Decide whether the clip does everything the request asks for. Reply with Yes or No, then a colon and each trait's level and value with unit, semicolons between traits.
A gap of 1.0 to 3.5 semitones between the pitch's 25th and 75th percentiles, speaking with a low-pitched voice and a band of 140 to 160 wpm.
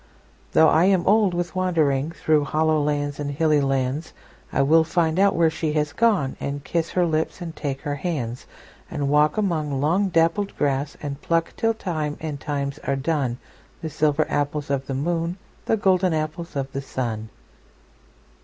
No: average, 3.0 semitones; medium, 155 Hz; average, 155 wpm